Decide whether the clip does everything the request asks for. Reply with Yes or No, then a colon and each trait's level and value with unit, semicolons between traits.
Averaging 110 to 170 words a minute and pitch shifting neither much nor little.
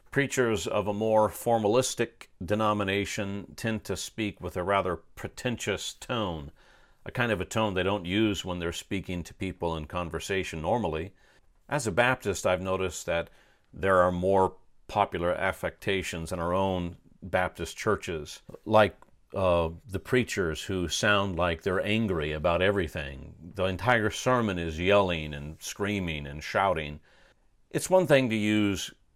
Yes: average, 145 wpm; average, 3.5 semitones